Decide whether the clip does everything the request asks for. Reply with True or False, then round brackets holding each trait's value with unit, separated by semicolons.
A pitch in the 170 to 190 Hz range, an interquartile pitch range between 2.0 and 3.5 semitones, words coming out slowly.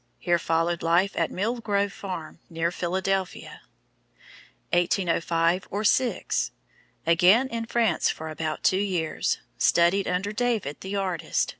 True (185 Hz; 3.2 semitones; 125 wpm)